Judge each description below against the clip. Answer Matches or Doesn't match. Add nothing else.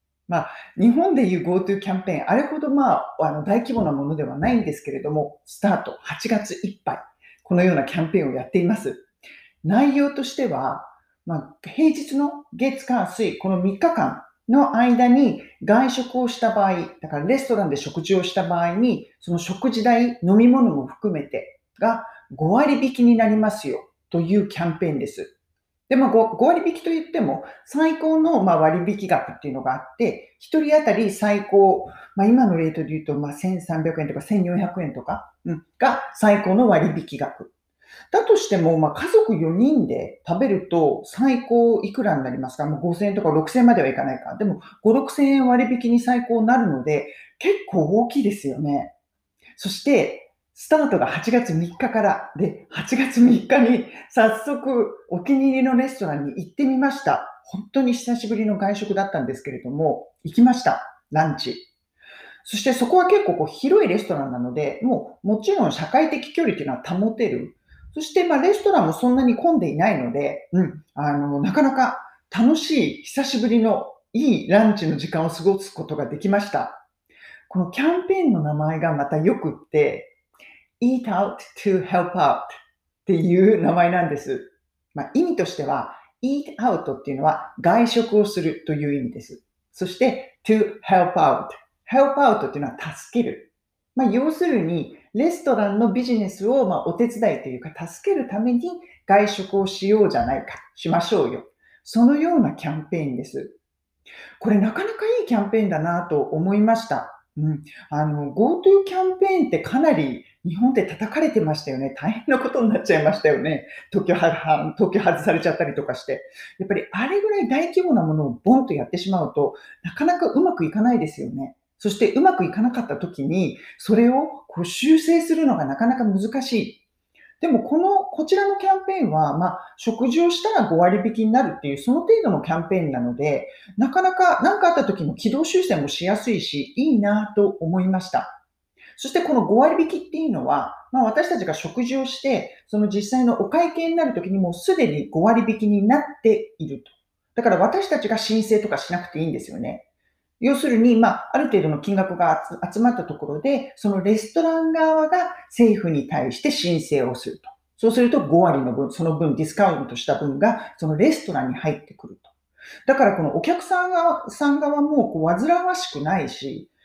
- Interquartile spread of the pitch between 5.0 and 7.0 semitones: Doesn't match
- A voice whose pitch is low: Doesn't match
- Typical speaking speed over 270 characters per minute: Matches